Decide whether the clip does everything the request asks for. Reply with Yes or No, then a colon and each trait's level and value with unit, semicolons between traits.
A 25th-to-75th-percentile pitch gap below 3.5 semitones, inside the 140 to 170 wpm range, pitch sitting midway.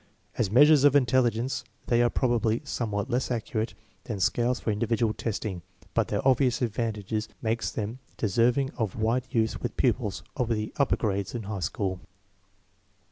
No: average, 2.7 semitones; average, 165 wpm; low, 115 Hz